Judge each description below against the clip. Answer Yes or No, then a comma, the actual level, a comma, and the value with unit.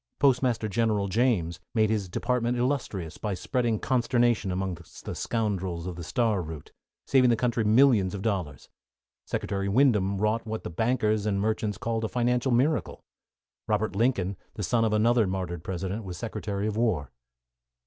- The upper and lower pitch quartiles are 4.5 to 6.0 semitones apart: No, average, 3.7 semitones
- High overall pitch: No, low, 110 Hz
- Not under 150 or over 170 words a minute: Yes, average, 160 wpm